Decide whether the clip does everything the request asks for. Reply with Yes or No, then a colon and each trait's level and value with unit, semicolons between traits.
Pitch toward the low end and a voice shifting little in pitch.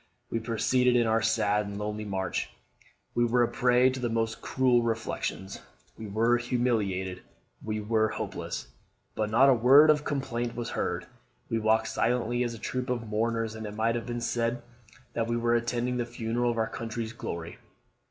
Yes: low, 115 Hz; narrow, 1.7 semitones